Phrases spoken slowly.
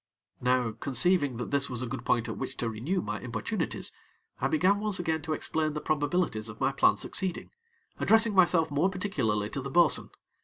No: average, 190 wpm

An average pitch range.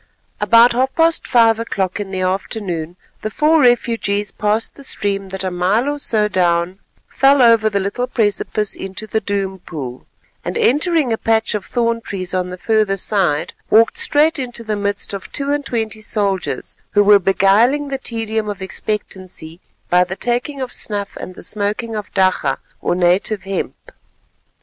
Yes: average, 3.6 semitones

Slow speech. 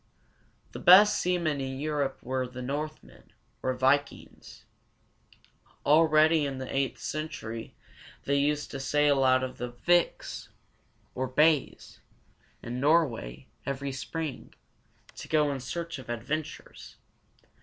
Yes: slow, 120 wpm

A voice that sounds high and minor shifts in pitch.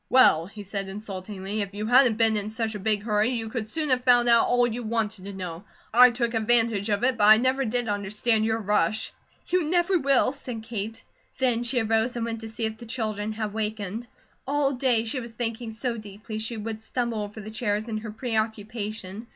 Yes: high, 220 Hz; narrow, 2.3 semitones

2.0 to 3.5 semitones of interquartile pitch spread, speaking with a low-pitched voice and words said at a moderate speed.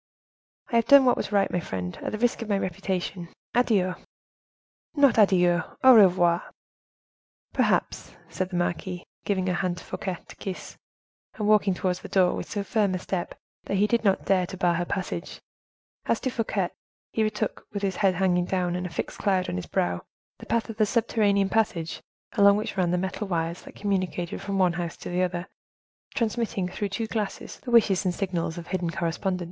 No: average, 3.0 semitones; high, 190 Hz; average, 195 wpm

